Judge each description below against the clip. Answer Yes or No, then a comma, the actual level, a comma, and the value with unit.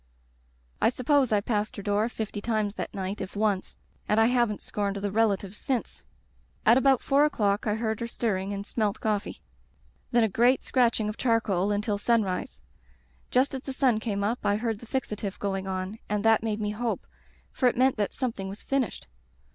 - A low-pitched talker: No, high, 215 Hz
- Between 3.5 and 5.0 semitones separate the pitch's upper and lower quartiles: No, average, 2.8 semitones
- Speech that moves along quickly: No, average, 195 wpm